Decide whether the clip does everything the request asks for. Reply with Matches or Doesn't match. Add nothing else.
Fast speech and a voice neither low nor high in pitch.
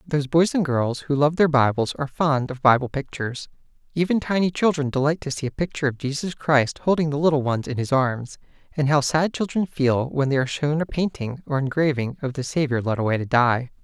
Matches